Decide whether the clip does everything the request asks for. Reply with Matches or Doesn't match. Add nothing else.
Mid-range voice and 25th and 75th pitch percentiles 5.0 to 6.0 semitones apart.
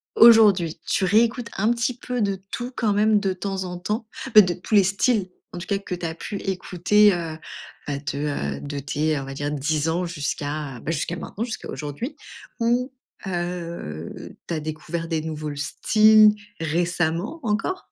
Matches